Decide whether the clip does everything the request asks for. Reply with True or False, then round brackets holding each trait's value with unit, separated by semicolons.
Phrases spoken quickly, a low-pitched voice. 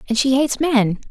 False (220 wpm; 250 Hz)